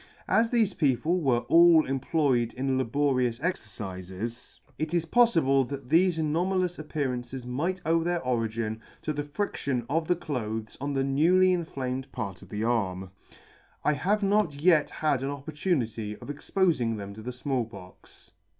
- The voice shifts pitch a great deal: Yes, wide, 5.7 semitones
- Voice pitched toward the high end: No, medium, 140 Hz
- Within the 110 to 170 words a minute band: Yes, average, 160 wpm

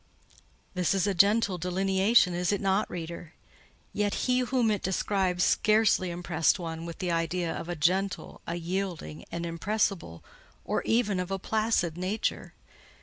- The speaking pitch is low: No, medium, 185 Hz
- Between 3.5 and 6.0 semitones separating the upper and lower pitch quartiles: No, average, 3.0 semitones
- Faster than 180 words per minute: No, average, 150 wpm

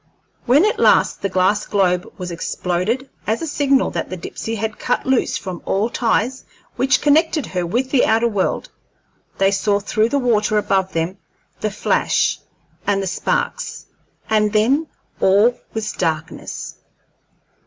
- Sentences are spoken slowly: No, average, 150 wpm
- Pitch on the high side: Yes, high, 215 Hz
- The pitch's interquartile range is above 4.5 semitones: Yes, average, 4.9 semitones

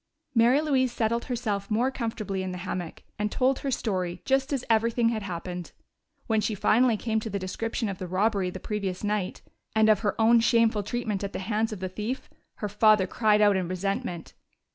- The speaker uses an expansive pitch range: No, average, 3.3 semitones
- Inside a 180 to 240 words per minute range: Yes, average, 200 wpm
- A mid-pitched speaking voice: No, high, 215 Hz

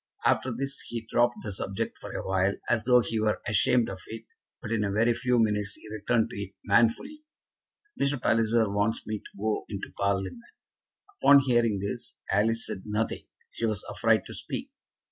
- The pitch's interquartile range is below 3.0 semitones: Yes, narrow, 2.6 semitones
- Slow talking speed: No, average, 185 wpm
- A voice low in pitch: Yes, low, 110 Hz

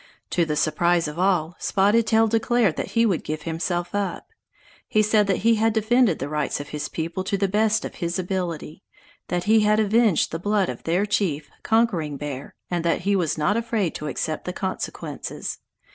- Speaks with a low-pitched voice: No, high, 190 Hz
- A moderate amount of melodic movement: Yes, average, 4.6 semitones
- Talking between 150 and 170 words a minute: No, average, 195 wpm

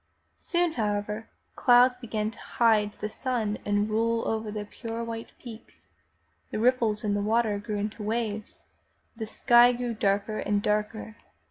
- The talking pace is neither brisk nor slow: Yes, average, 155 wpm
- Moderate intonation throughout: No, narrow, 2.0 semitones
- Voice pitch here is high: Yes, high, 220 Hz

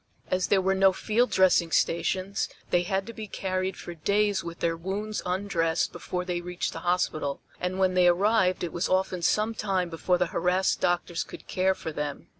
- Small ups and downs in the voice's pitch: Yes, narrow, 1.8 semitones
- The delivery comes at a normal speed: Yes, average, 195 wpm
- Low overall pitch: No, medium, 185 Hz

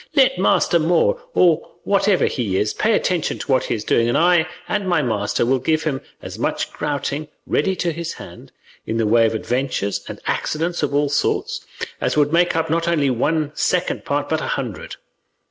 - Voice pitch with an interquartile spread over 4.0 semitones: Yes, average, 5.3 semitones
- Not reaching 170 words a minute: No, average, 195 wpm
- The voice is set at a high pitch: No, medium, 150 Hz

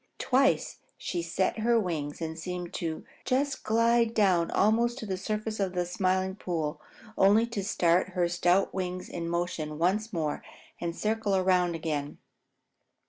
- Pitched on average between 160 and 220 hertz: Yes, medium, 185 Hz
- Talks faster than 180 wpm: No, average, 150 wpm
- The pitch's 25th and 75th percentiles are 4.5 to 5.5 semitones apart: No, average, 4.0 semitones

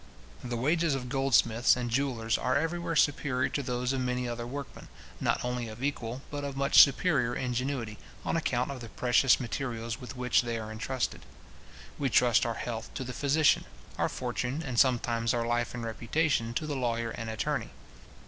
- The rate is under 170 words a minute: No, average, 180 wpm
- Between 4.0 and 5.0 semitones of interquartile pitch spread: No, average, 2.7 semitones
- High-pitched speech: No, low, 125 Hz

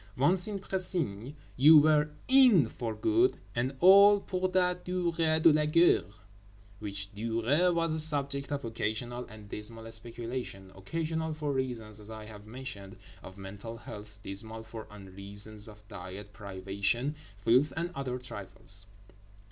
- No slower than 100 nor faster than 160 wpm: Yes, average, 140 wpm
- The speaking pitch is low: Yes, low, 120 Hz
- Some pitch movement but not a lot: No, wide, 7.2 semitones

